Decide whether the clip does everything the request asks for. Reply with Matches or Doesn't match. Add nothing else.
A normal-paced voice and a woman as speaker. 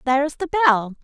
Matches